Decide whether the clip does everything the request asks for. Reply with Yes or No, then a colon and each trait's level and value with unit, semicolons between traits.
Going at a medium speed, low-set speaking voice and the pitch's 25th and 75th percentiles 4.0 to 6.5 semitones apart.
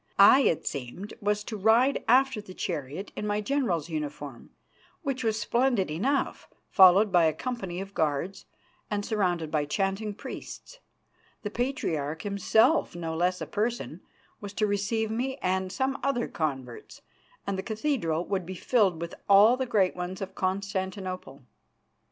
No: average, 150 wpm; high, 195 Hz; average, 4.3 semitones